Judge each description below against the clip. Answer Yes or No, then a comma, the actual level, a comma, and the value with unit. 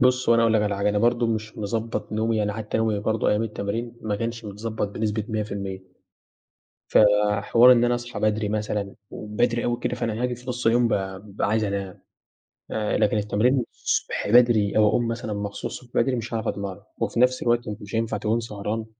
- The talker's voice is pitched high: No, low, 110 Hz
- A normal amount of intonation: No, narrow, 2.2 semitones